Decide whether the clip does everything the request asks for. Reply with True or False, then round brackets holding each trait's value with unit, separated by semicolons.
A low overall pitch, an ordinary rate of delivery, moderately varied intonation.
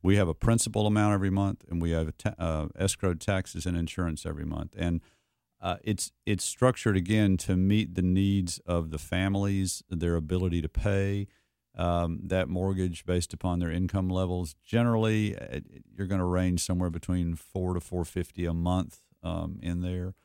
False (90 Hz; 175 wpm; 2.3 semitones)